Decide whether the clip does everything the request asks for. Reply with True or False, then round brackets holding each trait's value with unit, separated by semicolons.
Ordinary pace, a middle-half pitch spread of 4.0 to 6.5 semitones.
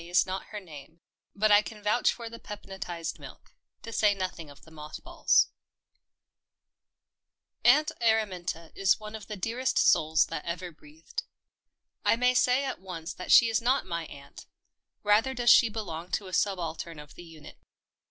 True (170 wpm; 5.2 semitones)